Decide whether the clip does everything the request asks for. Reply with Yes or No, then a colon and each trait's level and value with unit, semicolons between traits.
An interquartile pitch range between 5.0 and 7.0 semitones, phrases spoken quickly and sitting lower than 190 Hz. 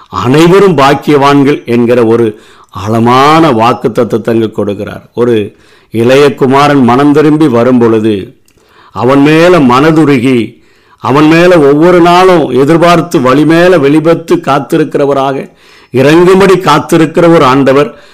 No: average, 5.3 semitones; average, 105 wpm; medium, 140 Hz